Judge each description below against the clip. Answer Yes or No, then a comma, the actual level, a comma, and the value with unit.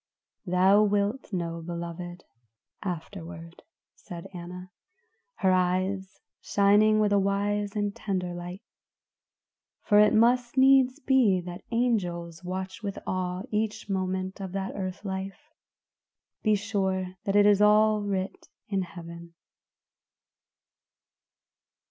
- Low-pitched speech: No, high, 195 Hz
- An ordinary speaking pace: No, slow, 110 wpm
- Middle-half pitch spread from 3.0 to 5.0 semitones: No, narrow, 2.5 semitones